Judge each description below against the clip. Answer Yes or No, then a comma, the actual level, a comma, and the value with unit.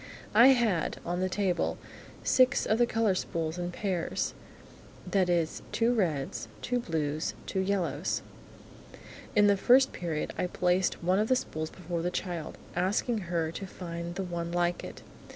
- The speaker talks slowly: No, average, 160 wpm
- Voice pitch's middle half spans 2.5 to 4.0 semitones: Yes, average, 3.3 semitones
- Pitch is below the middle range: No, medium, 180 Hz